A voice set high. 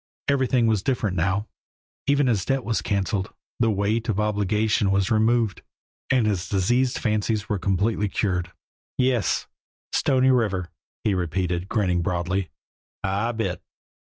No: low, 105 Hz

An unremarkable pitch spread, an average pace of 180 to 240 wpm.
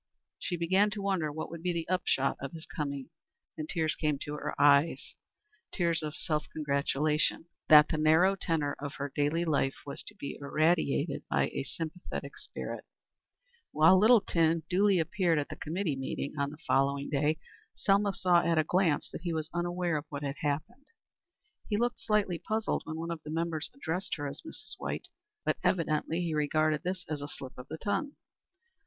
Yes: average, 3.2 semitones; average, 185 wpm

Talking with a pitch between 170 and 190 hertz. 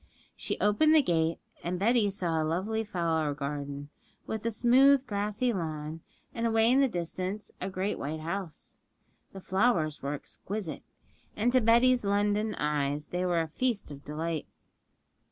Yes: medium, 185 Hz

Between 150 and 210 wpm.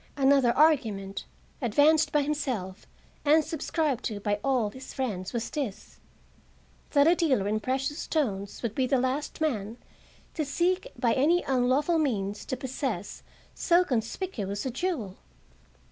No: average, 140 wpm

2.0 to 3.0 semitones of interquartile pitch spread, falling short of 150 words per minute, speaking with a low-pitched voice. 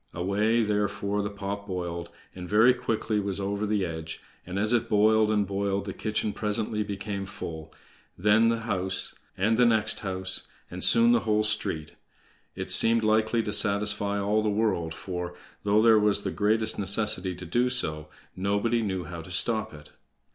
No: narrow, 2.5 semitones; average, 175 wpm; low, 105 Hz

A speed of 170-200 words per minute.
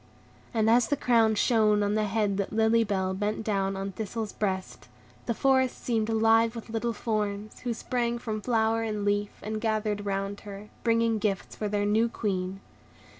Yes: average, 175 wpm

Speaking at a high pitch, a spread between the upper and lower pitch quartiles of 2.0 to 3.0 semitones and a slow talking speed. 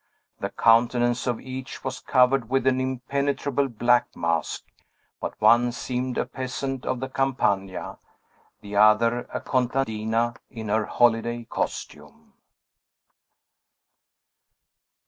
No: low, 120 Hz; narrow, 2.4 semitones; slow, 105 wpm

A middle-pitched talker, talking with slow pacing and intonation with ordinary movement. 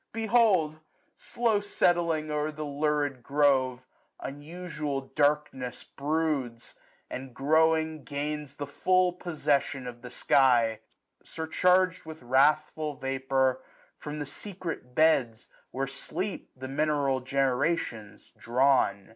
Yes: medium, 145 Hz; slow, 110 wpm; average, 3.2 semitones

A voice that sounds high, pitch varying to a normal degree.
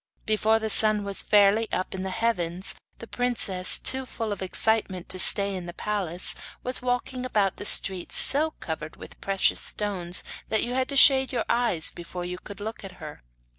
Yes: high, 205 Hz; average, 3.9 semitones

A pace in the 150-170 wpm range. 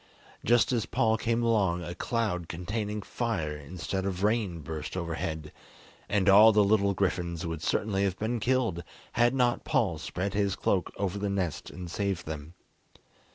Yes: average, 160 wpm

